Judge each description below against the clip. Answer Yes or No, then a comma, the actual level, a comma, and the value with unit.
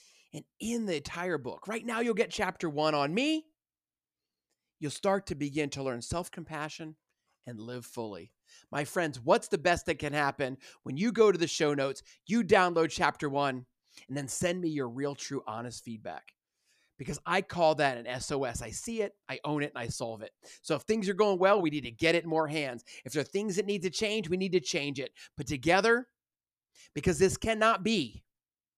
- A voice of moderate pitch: Yes, medium, 160 Hz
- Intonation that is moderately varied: No, wide, 5.9 semitones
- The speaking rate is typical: No, fast, 210 wpm